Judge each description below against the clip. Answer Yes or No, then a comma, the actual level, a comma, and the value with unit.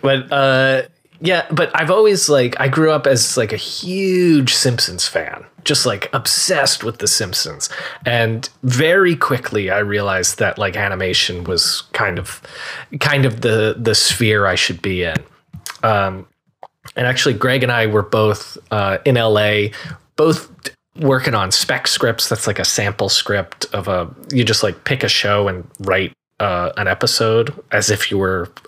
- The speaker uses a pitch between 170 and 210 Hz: No, low, 120 Hz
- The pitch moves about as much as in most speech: Yes, average, 4.7 semitones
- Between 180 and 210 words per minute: No, average, 165 wpm